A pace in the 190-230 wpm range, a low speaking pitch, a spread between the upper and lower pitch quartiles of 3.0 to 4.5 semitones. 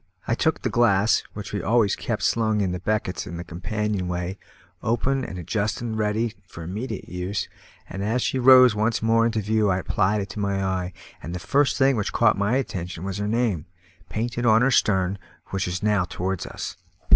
Yes: average, 195 wpm; low, 105 Hz; average, 3.5 semitones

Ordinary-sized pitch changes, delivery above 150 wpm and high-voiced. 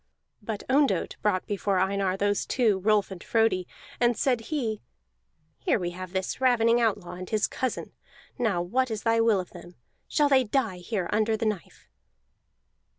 Yes: average, 3.7 semitones; average, 165 wpm; high, 215 Hz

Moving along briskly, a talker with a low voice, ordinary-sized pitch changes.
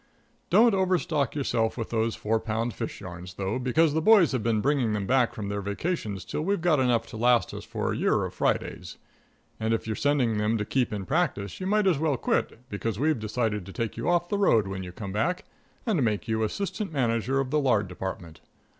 No: fast, 220 wpm; low, 115 Hz; wide, 6.2 semitones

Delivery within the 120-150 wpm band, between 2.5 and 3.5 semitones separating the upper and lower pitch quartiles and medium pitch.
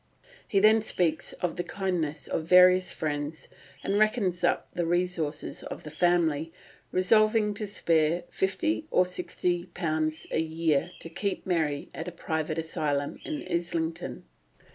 Yes: average, 140 wpm; average, 2.8 semitones; medium, 175 Hz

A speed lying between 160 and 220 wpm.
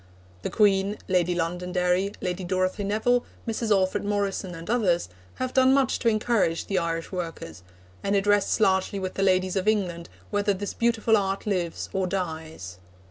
Yes: average, 165 wpm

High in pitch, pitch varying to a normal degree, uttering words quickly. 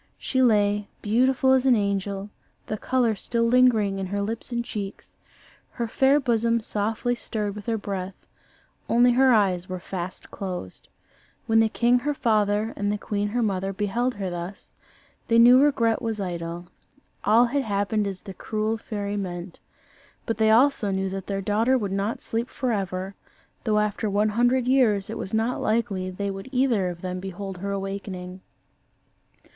No: high, 210 Hz; average, 3.2 semitones; average, 170 wpm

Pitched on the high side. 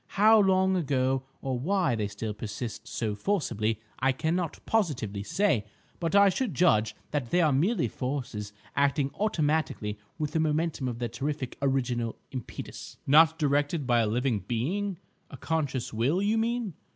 No: medium, 140 Hz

